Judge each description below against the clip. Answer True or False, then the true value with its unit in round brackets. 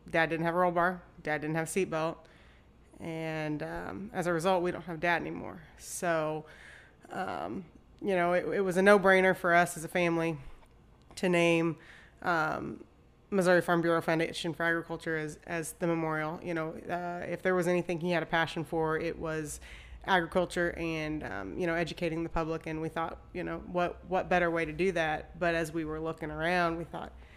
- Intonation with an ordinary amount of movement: False (1.5 semitones)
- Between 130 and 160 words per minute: False (200 wpm)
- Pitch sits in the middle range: True (165 Hz)